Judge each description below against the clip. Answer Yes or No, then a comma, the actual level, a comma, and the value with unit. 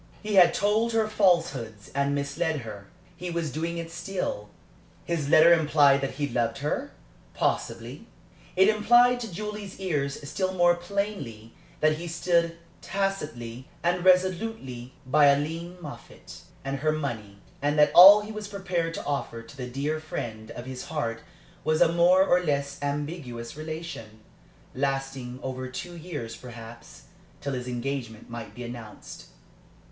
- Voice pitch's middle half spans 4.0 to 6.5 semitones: Yes, wide, 5.5 semitones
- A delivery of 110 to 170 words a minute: Yes, average, 150 wpm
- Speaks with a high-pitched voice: No, medium, 150 Hz